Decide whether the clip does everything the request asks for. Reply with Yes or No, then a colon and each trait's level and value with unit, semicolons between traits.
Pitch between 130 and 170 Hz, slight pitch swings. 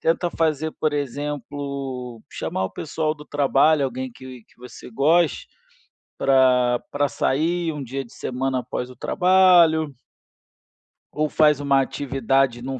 No: medium, 140 Hz; average, 3.1 semitones